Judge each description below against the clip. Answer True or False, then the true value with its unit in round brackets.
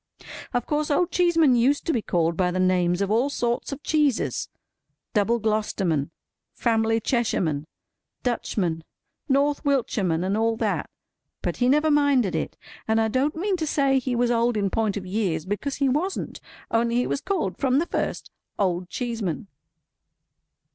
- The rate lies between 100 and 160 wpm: True (155 wpm)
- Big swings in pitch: True (6.2 semitones)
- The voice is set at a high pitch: True (235 Hz)